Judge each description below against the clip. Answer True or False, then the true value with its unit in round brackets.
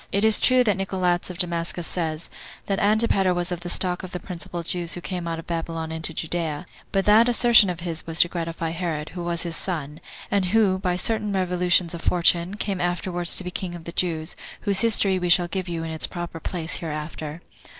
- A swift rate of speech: True (215 wpm)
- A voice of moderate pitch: True (175 Hz)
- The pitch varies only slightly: True (2.1 semitones)